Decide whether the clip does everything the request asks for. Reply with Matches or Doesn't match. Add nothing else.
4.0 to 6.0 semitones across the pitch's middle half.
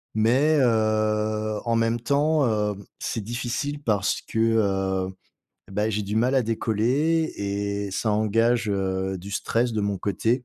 Doesn't match